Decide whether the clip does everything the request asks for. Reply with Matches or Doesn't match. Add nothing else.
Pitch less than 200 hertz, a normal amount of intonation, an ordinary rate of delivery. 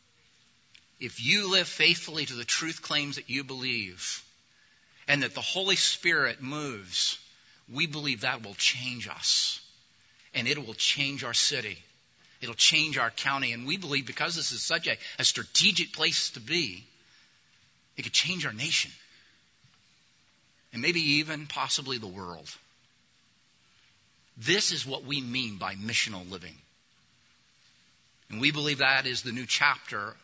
Matches